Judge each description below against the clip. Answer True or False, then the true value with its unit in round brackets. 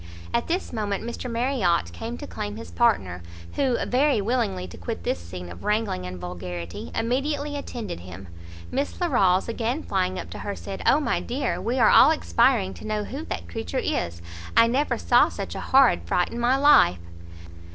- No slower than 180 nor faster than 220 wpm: True (185 wpm)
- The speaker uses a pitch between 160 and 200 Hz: False (220 Hz)